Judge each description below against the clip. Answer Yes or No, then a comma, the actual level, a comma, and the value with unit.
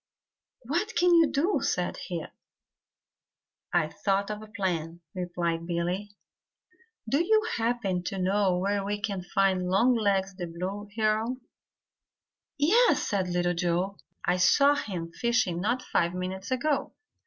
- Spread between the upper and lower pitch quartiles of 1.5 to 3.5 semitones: No, average, 4.8 semitones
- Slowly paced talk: Yes, slow, 130 wpm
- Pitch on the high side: Yes, high, 195 Hz